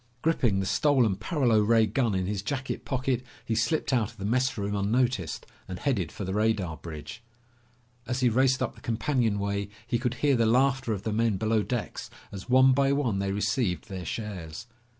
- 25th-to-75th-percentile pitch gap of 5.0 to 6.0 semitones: No, average, 4.2 semitones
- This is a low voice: Yes, low, 110 Hz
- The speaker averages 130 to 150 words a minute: No, average, 190 wpm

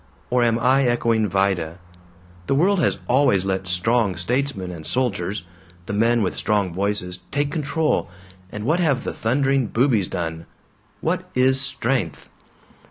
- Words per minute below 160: Yes, average, 145 wpm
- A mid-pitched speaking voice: No, low, 115 Hz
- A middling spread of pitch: No, wide, 5.9 semitones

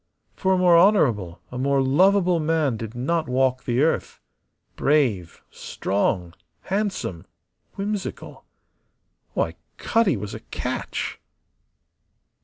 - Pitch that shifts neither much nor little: No, wide, 7.8 semitones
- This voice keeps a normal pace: No, slow, 105 wpm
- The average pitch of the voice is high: No, medium, 140 Hz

